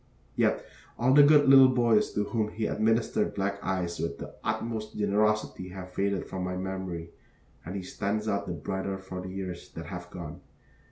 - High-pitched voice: No, low, 100 Hz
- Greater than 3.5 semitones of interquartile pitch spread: No, average, 2.8 semitones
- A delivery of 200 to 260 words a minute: No, average, 180 wpm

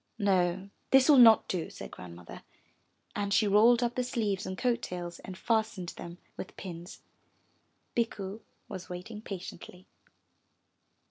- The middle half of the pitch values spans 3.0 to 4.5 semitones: Yes, average, 4.1 semitones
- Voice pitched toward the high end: Yes, high, 200 Hz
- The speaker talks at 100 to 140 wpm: Yes, slow, 135 wpm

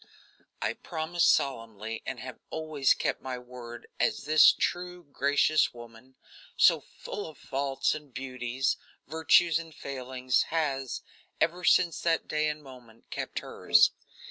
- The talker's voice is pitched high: No, medium, 140 Hz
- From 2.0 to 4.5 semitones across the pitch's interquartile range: Yes, average, 3.9 semitones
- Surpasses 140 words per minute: No, slow, 135 wpm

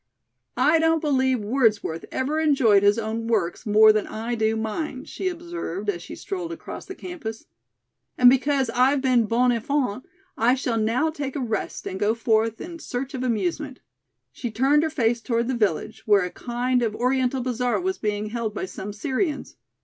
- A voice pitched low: No, high, 245 Hz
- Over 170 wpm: Yes, average, 180 wpm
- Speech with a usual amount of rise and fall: Yes, average, 3.9 semitones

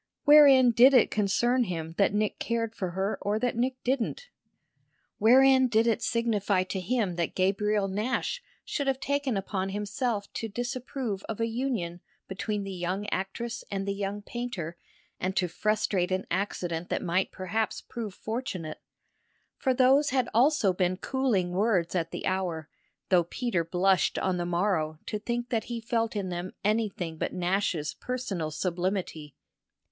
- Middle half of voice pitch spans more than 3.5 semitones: Yes, average, 4.5 semitones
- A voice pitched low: No, high, 205 Hz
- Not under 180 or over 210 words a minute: No, average, 160 wpm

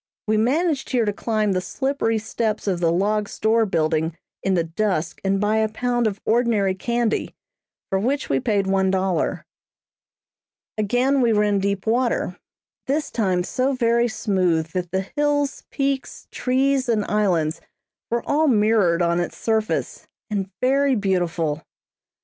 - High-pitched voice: Yes, high, 215 Hz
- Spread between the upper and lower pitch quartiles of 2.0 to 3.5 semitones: No, average, 4.3 semitones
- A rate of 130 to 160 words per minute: Yes, average, 150 wpm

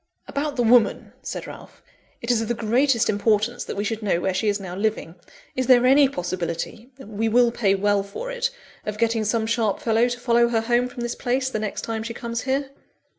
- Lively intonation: No, narrow, 2.6 semitones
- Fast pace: Yes, fast, 220 wpm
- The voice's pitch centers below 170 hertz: No, high, 230 Hz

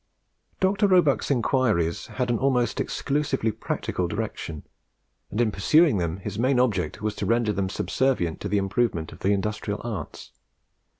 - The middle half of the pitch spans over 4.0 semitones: Yes, average, 4.8 semitones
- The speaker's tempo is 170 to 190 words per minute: No, average, 155 wpm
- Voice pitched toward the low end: Yes, low, 110 Hz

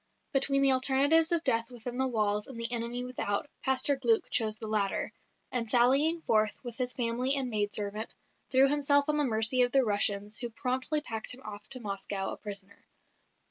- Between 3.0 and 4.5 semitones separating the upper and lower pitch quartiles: Yes, average, 3.8 semitones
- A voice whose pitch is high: Yes, high, 245 Hz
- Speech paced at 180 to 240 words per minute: Yes, average, 190 wpm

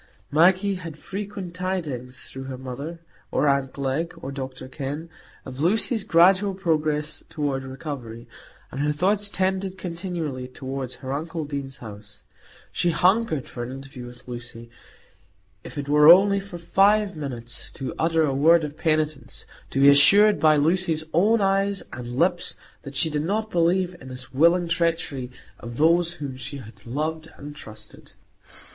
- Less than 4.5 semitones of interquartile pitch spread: No, average, 5.0 semitones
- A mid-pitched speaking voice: Yes, medium, 155 Hz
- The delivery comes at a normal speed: Yes, average, 155 wpm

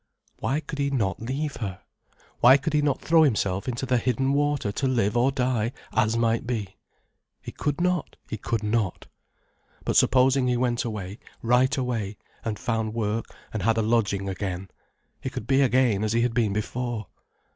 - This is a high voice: No, low, 120 Hz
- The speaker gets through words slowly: No, average, 180 wpm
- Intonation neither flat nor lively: Yes, average, 3.6 semitones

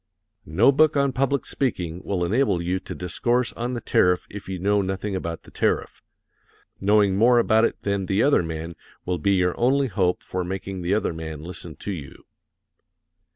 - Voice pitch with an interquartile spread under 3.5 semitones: No, average, 4.8 semitones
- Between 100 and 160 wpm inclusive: No, average, 185 wpm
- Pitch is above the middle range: No, very low, 95 Hz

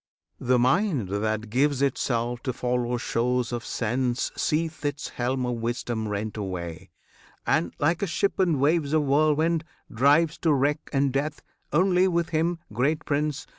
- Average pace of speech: Yes, average, 155 wpm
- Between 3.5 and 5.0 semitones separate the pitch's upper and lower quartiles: Yes, average, 4.5 semitones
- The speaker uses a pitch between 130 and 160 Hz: Yes, low, 135 Hz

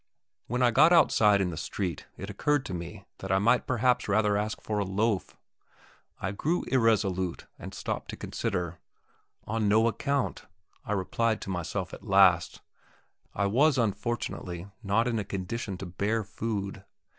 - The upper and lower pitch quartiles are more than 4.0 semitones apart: No, average, 3.3 semitones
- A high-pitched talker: No, low, 105 Hz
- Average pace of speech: Yes, average, 160 wpm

